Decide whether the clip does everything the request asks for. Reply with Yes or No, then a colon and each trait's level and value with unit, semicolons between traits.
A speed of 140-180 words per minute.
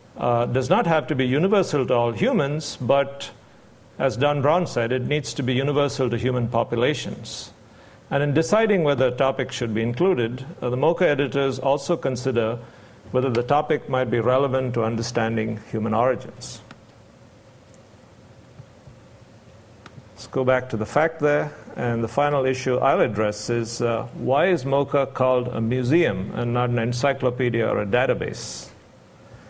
Yes: average, 155 wpm